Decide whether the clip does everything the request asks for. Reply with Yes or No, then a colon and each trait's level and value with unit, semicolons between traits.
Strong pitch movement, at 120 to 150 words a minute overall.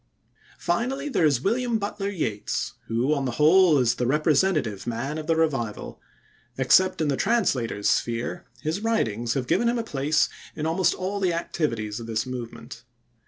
No: wide, 7.9 semitones; average, 165 wpm